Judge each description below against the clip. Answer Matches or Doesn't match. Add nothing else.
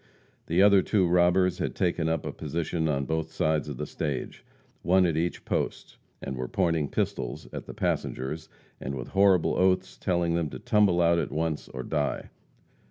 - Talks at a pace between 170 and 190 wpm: Matches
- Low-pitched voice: Matches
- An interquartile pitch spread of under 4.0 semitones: Matches